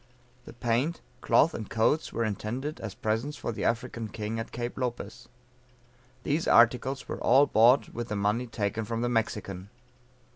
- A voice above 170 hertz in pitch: No, low, 115 Hz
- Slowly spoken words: No, average, 160 wpm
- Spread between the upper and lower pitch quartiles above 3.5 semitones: No, narrow, 2.6 semitones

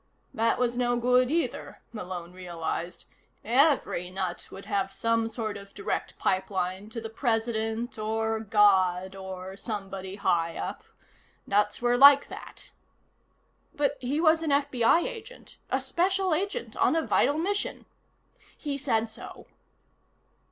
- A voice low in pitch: No, high, 225 Hz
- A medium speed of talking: No, slow, 130 wpm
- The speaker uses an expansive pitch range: Yes, wide, 6.3 semitones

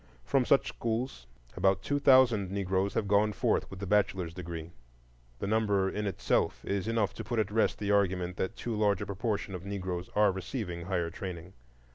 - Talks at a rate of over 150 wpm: Yes, average, 185 wpm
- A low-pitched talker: Yes, low, 100 Hz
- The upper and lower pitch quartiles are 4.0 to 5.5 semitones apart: No, narrow, 2.6 semitones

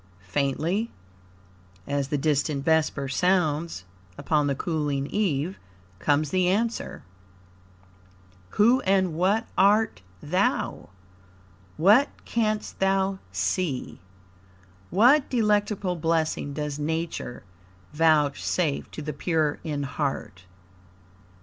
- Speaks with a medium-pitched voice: Yes, medium, 160 Hz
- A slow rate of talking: Yes, slow, 90 wpm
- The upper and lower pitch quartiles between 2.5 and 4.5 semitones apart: No, average, 5.0 semitones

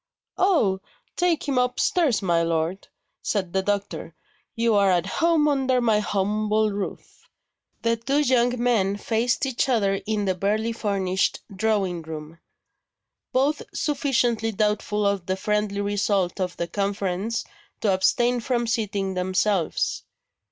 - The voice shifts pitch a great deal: No, average, 3.8 semitones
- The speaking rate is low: Yes, slow, 130 wpm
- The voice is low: No, high, 210 Hz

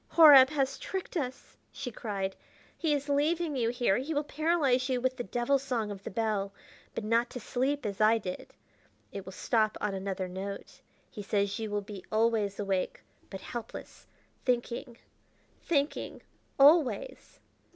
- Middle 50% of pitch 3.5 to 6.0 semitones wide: Yes, wide, 5.4 semitones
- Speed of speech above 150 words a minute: Yes, average, 160 wpm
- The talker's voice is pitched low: No, high, 240 Hz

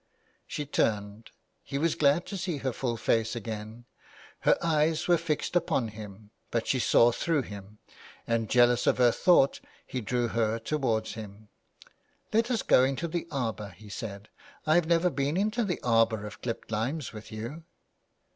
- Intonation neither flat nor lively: No, wide, 6.1 semitones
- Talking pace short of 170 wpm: No, average, 175 wpm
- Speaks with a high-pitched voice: No, low, 120 Hz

